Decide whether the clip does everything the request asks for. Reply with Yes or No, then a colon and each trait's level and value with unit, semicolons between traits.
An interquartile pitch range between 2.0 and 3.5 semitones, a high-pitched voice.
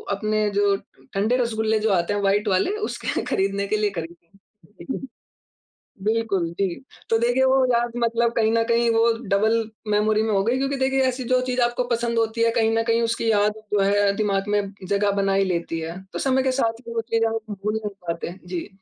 Yes: average, 2.8 semitones; high, 220 Hz